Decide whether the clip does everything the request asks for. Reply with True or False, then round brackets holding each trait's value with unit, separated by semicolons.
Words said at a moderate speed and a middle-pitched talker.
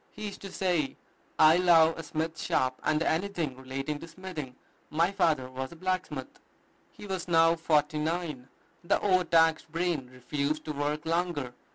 True (160 wpm; 160 Hz)